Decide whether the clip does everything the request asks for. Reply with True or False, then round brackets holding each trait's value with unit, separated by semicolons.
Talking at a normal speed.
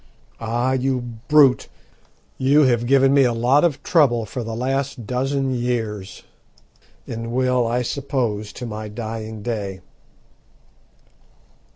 False (120 wpm)